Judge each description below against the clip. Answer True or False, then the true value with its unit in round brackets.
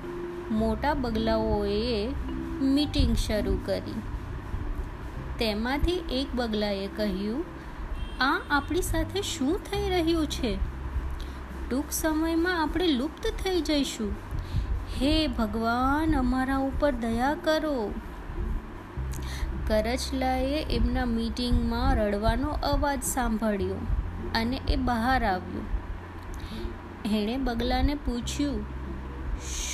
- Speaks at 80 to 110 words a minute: True (85 wpm)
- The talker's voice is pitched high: True (230 Hz)